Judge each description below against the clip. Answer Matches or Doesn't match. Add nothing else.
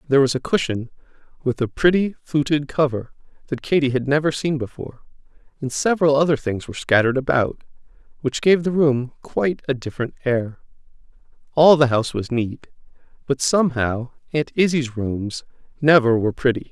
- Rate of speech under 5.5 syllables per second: Doesn't match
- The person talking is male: Matches